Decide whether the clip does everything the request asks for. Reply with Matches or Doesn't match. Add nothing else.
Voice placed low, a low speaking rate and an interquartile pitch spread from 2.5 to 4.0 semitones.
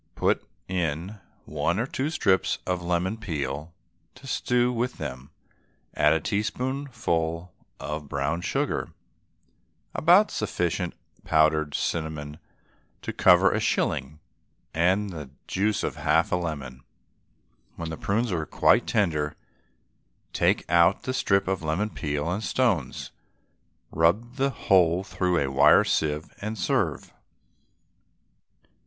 Doesn't match